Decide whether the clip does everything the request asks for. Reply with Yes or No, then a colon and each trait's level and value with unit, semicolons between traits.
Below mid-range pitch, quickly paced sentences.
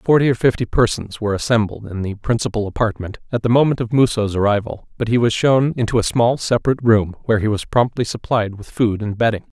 Yes: low, 110 Hz; fast, 215 wpm